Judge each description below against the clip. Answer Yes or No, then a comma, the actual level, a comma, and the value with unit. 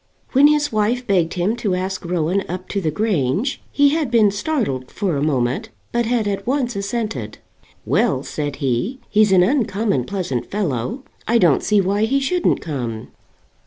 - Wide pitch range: Yes, wide, 6.5 semitones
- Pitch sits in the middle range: No, high, 200 Hz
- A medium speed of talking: Yes, average, 170 wpm